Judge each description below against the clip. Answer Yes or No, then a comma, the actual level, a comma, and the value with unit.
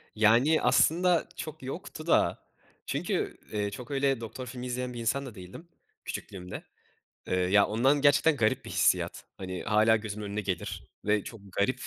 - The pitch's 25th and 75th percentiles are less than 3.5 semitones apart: No, average, 4.8 semitones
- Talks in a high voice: No, low, 115 Hz